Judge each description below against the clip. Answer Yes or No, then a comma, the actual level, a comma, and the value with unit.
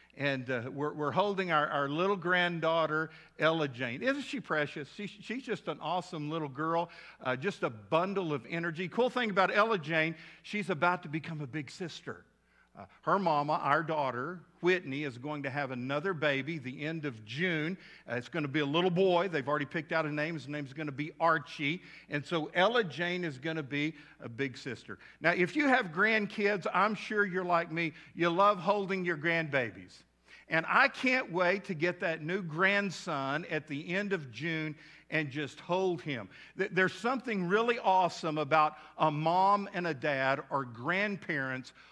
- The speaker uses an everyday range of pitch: Yes, average, 3.9 semitones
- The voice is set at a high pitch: No, medium, 165 Hz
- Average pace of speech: Yes, average, 190 wpm